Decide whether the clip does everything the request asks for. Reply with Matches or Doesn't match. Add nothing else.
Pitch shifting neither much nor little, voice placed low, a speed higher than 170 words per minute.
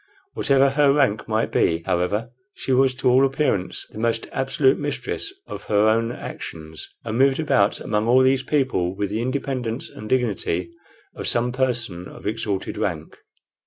Doesn't match